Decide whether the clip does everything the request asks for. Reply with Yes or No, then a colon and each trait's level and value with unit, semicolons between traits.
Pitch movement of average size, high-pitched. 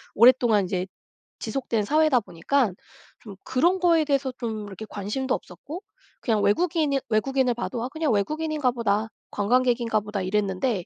Yes: average, 5.0 semitones; high, 240 Hz